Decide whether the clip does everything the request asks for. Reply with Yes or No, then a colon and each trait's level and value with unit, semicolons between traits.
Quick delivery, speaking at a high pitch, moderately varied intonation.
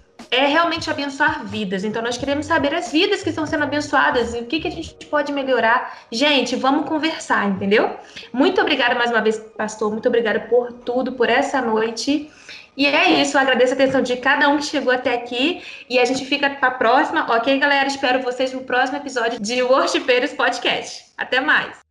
Yes: fast, 200 wpm; very high, 265 Hz; average, 3.4 semitones